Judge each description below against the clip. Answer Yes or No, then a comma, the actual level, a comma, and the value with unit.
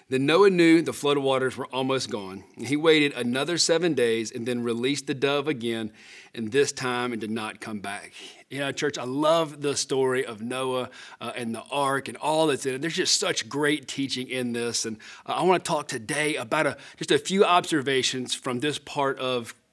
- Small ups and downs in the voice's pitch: No, average, 3.4 semitones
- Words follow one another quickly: Yes, fast, 210 wpm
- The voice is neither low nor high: No, low, 130 Hz